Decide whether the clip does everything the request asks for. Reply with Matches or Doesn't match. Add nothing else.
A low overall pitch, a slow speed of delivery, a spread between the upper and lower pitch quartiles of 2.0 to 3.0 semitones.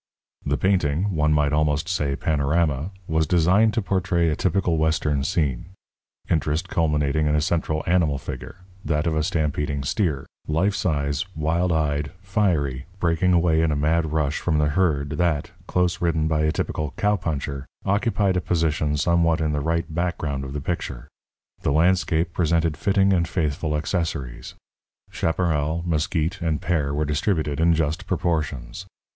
Doesn't match